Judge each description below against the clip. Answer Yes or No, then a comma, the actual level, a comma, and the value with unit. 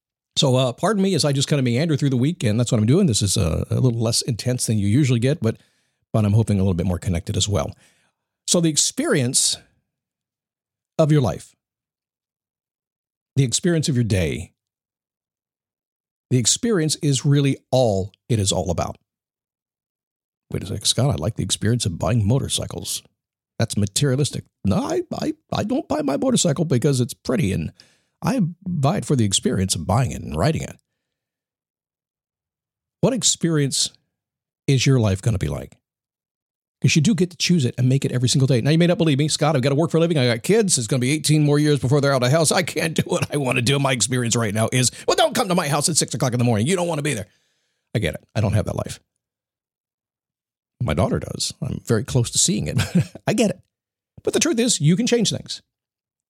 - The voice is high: No, low, 135 Hz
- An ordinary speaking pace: No, fast, 220 wpm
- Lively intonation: Yes, wide, 5.7 semitones